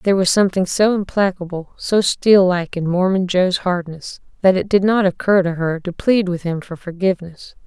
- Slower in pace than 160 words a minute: No, average, 195 wpm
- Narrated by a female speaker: Yes, female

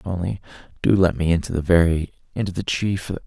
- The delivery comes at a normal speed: Yes, average, 185 wpm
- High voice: No, very low, 90 Hz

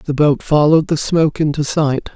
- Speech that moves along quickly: No, average, 195 wpm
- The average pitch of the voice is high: No, medium, 150 Hz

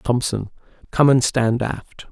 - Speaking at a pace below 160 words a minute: Yes, average, 140 wpm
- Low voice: Yes, low, 125 Hz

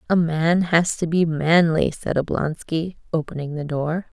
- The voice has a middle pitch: Yes, medium, 165 Hz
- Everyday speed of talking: Yes, average, 160 wpm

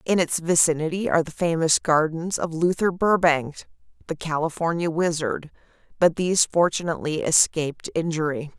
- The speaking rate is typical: No, slow, 125 wpm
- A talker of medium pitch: Yes, medium, 165 Hz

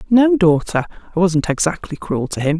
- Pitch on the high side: No, medium, 175 Hz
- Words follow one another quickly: No, average, 185 wpm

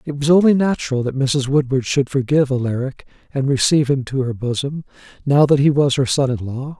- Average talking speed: No, fast, 210 wpm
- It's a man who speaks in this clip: Yes, male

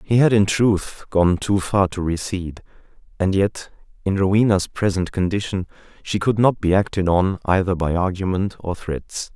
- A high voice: No, very low, 95 Hz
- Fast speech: No, average, 165 wpm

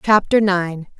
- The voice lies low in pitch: No, high, 190 Hz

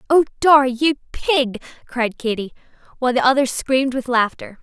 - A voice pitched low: No, very high, 260 Hz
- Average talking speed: Yes, average, 155 wpm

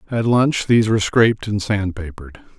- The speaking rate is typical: Yes, average, 185 wpm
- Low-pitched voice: Yes, low, 105 Hz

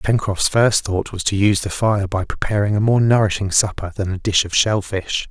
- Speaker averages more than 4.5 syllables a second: Yes, 5.2 syllables/s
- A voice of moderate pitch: No, low, 100 Hz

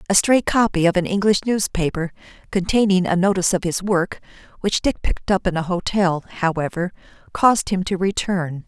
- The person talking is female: Yes, female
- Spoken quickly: No, average, 175 wpm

